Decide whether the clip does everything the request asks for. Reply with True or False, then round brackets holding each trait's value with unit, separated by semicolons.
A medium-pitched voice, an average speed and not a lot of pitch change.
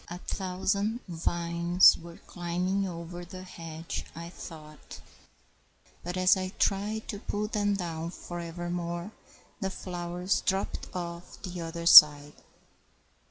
False (175 Hz; 120 wpm; 2.0 semitones)